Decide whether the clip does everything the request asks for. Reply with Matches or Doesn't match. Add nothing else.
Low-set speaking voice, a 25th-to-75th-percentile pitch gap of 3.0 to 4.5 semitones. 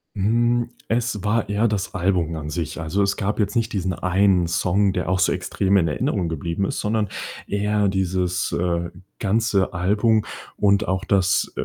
Doesn't match